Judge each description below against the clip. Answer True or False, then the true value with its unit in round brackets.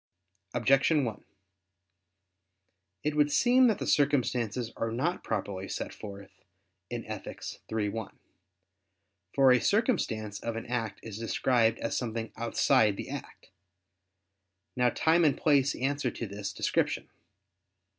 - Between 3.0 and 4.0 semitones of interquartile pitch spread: False (4.5 semitones)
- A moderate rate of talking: False (125 wpm)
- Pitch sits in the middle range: False (120 Hz)